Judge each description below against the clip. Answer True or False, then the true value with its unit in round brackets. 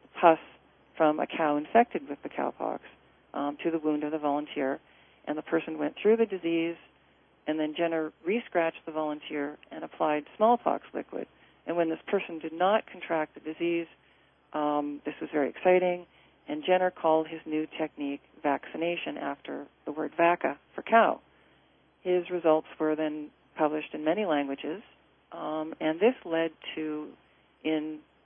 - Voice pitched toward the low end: False (160 Hz)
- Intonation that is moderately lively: False (1.9 semitones)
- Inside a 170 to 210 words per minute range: False (155 wpm)